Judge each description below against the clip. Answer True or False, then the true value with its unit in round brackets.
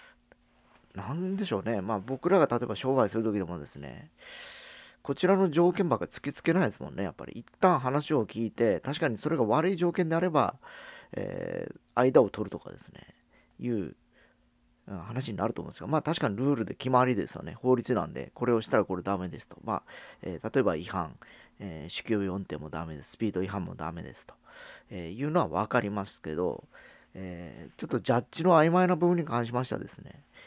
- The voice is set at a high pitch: False (125 Hz)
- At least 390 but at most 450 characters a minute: True (395 characters per minute)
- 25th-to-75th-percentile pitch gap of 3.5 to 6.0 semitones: False (8.5 semitones)